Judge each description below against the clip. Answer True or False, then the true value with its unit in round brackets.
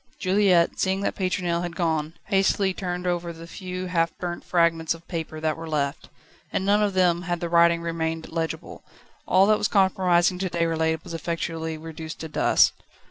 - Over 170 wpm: True (180 wpm)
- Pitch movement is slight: True (2.1 semitones)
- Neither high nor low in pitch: True (170 Hz)